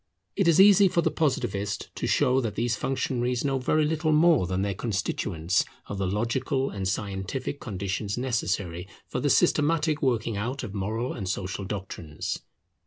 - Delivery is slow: No, average, 165 wpm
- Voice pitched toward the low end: Yes, low, 115 Hz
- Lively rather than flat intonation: Yes, wide, 5.8 semitones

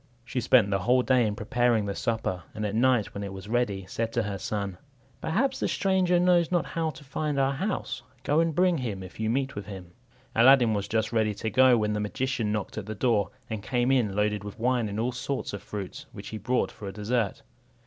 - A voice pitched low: Yes, low, 115 Hz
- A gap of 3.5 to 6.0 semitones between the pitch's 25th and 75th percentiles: Yes, average, 4.1 semitones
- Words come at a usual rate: No, fast, 230 wpm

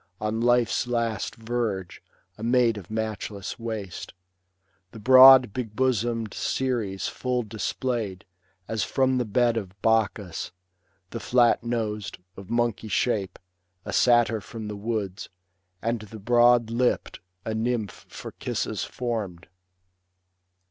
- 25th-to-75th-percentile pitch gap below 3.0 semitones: Yes, narrow, 2.4 semitones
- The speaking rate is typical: No, slow, 120 wpm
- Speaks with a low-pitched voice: Yes, low, 115 Hz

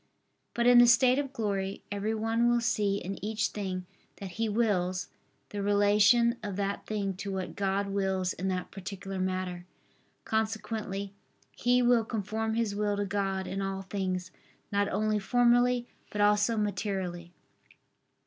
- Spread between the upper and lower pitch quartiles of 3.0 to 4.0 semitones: No, narrow, 2.5 semitones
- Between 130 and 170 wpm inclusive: Yes, average, 150 wpm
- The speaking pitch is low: No, high, 205 Hz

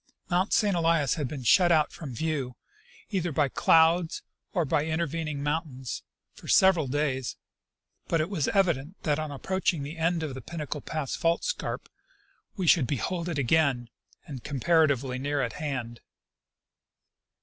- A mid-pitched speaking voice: Yes, medium, 155 Hz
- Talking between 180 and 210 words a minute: No, average, 150 wpm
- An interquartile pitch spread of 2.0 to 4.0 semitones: Yes, average, 3.4 semitones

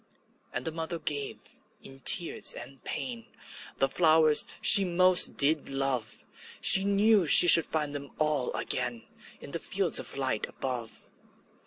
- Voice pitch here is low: No, medium, 150 Hz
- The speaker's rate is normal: Yes, average, 150 wpm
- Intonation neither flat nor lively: Yes, average, 4.1 semitones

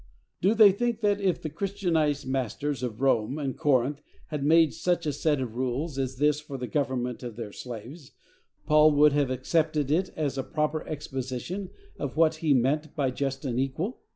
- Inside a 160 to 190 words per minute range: Yes, average, 185 wpm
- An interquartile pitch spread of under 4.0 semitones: Yes, average, 3.4 semitones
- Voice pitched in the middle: Yes, medium, 145 Hz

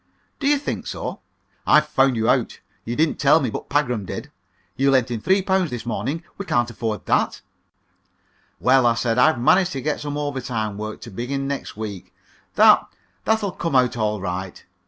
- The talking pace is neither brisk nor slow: Yes, average, 190 wpm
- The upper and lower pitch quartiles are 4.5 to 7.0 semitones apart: Yes, average, 4.8 semitones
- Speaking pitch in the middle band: No, low, 130 Hz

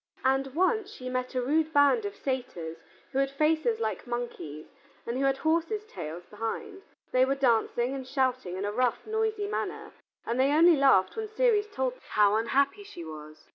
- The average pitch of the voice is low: No, very high, 265 Hz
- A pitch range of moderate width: No, wide, 5.7 semitones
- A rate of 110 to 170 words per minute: No, average, 185 wpm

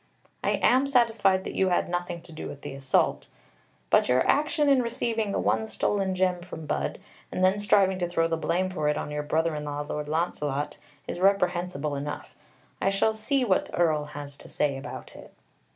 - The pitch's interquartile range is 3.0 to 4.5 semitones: No, average, 5.0 semitones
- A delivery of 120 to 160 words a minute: No, average, 200 wpm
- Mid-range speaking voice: Yes, medium, 175 Hz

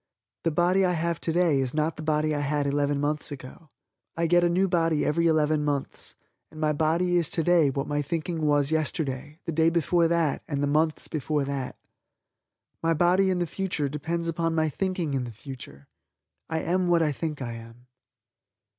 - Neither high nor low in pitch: Yes, medium, 155 Hz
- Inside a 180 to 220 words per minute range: Yes, average, 190 wpm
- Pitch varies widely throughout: No, average, 2.7 semitones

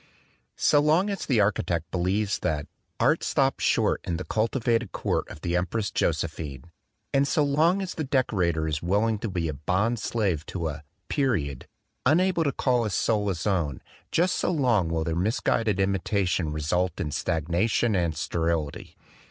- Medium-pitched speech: No, very low, 95 Hz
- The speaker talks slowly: No, average, 170 wpm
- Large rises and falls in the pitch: Yes, wide, 6.4 semitones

